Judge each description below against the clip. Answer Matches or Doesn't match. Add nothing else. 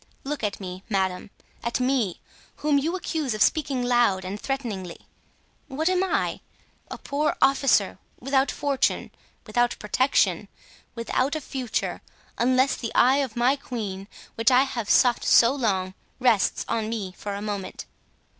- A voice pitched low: Doesn't match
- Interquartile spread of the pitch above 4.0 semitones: Matches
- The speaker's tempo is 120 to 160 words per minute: Matches